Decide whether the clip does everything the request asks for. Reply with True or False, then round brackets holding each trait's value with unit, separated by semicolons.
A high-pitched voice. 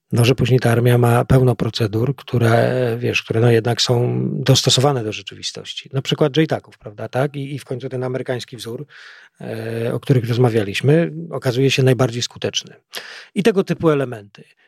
False (125 Hz)